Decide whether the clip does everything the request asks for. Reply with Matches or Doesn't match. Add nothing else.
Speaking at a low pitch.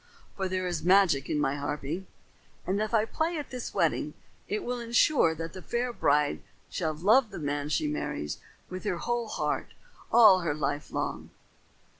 Doesn't match